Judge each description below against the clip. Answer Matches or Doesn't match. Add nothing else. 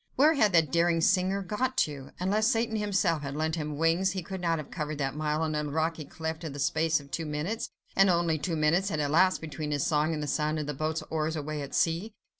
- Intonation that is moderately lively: Matches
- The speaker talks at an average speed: Doesn't match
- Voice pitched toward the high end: Doesn't match